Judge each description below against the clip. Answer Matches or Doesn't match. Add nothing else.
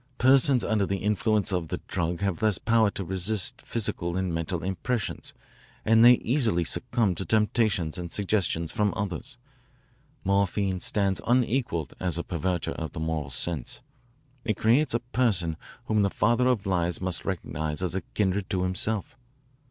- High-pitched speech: Doesn't match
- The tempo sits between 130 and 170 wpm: Matches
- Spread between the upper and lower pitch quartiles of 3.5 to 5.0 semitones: Matches